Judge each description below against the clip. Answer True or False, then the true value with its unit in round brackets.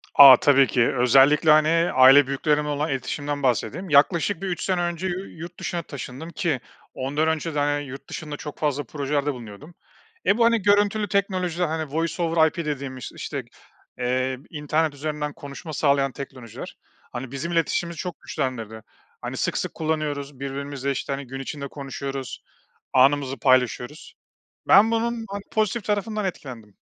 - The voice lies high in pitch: False (145 Hz)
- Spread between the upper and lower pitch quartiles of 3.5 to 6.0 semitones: True (3.9 semitones)